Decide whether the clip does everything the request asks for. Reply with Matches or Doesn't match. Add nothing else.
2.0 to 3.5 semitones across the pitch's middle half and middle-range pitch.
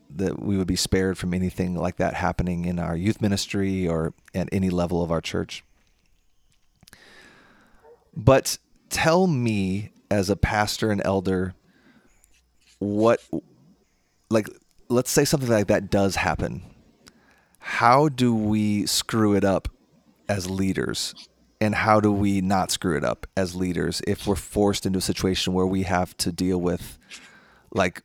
Doesn't match